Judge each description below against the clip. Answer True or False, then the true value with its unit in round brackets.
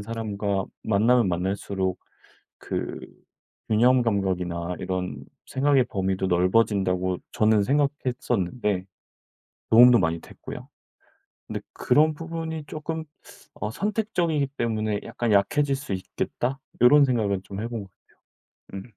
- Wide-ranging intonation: True (5.8 semitones)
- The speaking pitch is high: False (110 Hz)